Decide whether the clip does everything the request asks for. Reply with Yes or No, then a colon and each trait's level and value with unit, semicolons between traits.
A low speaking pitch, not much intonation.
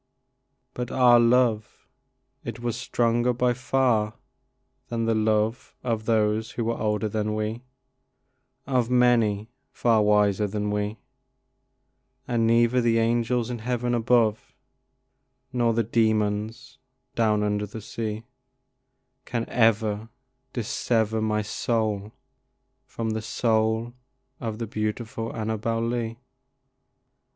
Yes: low, 115 Hz; narrow, 1.7 semitones